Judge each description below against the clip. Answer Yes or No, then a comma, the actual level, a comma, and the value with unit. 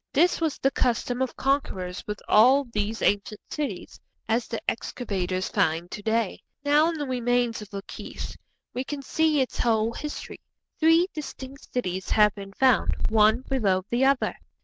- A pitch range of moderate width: Yes, average, 4.6 semitones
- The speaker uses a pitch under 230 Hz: No, high, 240 Hz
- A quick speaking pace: No, average, 160 wpm